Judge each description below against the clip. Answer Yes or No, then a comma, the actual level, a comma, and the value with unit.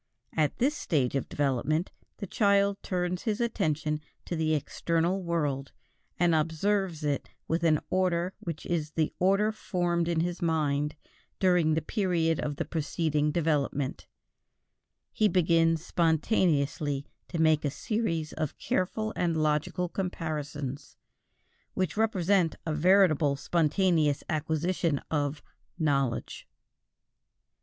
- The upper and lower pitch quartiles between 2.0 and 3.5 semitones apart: Yes, average, 3.2 semitones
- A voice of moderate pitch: Yes, medium, 165 Hz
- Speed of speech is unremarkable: No, slow, 120 wpm